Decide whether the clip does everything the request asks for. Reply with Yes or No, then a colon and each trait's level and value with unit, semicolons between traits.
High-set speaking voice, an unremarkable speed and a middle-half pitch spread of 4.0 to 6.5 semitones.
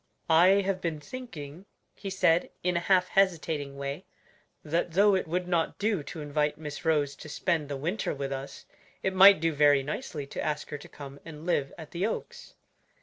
No: medium, 160 Hz; average, 195 wpm; average, 4.3 semitones